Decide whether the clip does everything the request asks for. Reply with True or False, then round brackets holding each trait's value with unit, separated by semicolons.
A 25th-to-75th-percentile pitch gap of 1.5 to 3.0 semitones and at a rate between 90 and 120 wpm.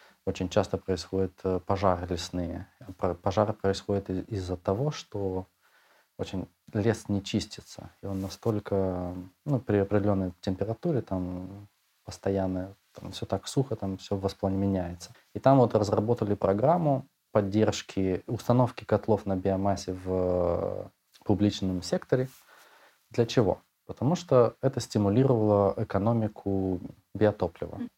True (2.7 semitones; 110 wpm)